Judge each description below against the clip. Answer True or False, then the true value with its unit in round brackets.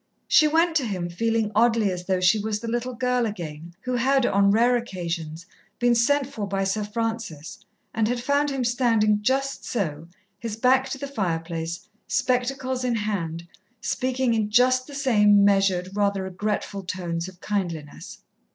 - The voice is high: True (215 Hz)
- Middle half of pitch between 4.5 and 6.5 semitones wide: True (5.1 semitones)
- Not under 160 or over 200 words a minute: True (165 wpm)